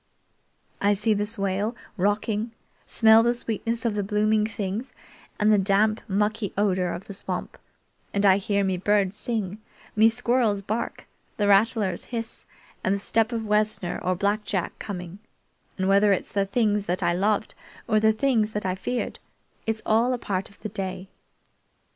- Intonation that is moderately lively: No, narrow, 2.0 semitones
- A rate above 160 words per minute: Yes, average, 170 wpm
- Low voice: No, high, 210 Hz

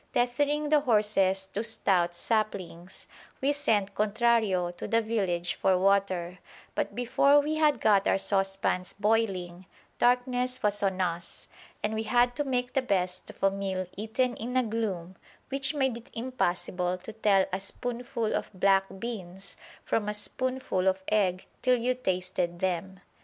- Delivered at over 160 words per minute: No, average, 155 wpm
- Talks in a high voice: Yes, high, 210 Hz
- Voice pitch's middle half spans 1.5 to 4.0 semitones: No, average, 4.6 semitones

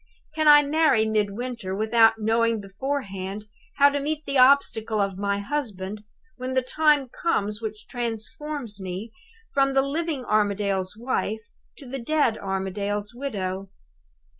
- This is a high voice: Yes, high, 225 Hz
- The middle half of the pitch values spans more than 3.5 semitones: Yes, average, 5.3 semitones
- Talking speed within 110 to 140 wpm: Yes, slow, 135 wpm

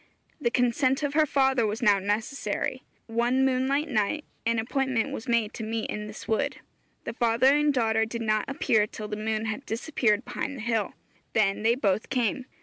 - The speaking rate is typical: Yes, average, 185 wpm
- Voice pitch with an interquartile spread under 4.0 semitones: Yes, average, 3.5 semitones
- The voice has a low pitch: No, high, 230 Hz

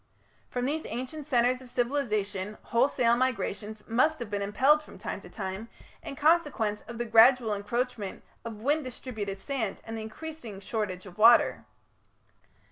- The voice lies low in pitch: No, high, 235 Hz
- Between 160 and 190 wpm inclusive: No, average, 150 wpm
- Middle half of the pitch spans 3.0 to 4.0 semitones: Yes, average, 3.7 semitones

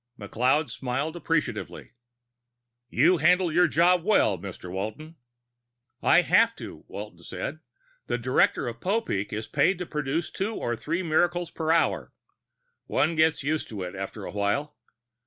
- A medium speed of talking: Yes, average, 145 wpm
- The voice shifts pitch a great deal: Yes, wide, 7.5 semitones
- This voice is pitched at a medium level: Yes, medium, 150 Hz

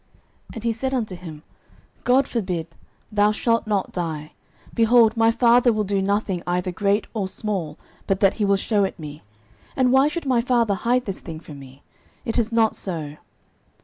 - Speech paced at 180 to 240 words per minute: Yes, average, 185 wpm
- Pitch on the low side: No, high, 205 Hz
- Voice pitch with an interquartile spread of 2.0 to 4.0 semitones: No, average, 4.4 semitones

